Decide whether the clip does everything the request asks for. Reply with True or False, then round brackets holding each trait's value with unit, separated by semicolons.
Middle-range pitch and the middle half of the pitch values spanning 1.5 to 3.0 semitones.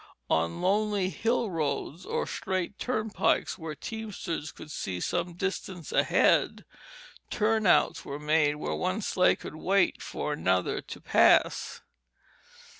False (180 Hz; 5.4 semitones)